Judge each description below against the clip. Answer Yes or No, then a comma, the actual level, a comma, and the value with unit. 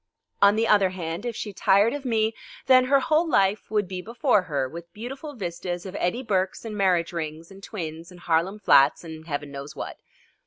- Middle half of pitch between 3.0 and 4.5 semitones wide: No, average, 4.9 semitones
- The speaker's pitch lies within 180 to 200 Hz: Yes, high, 190 Hz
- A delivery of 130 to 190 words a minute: No, average, 200 wpm